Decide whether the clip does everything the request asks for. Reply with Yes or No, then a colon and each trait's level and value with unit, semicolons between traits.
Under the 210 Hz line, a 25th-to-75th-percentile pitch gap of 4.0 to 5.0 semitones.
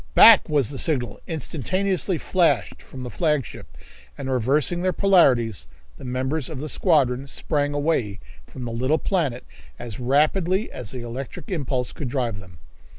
Yes: medium, 140 Hz; average, 4.6 semitones